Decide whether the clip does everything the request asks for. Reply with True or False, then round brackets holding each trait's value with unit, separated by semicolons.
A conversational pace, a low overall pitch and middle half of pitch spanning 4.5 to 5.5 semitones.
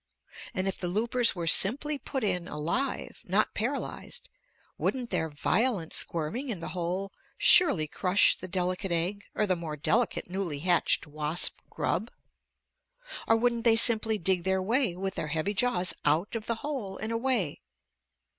False (155 wpm; 190 Hz; 5.1 semitones)